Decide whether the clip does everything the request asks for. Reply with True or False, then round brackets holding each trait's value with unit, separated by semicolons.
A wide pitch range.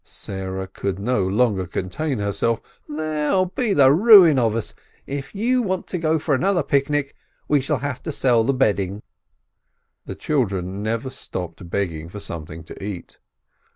True (7.8 semitones)